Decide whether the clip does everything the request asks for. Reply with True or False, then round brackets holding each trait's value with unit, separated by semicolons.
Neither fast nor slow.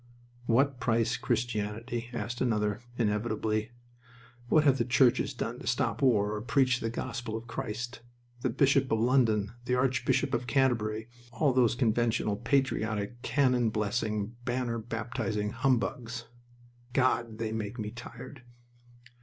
False (130 wpm)